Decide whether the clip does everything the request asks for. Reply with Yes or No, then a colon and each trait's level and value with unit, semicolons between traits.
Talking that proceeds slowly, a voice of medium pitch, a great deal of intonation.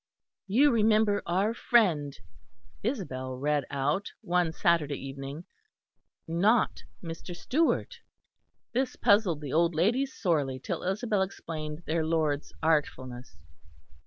Yes: slow, 105 wpm; medium, 170 Hz; wide, 6.1 semitones